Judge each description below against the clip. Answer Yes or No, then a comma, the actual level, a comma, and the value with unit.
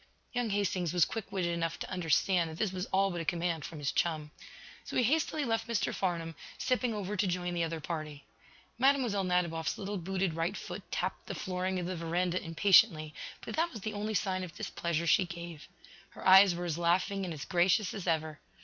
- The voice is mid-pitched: Yes, medium, 180 Hz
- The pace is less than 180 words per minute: No, fast, 205 wpm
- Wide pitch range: No, average, 3.0 semitones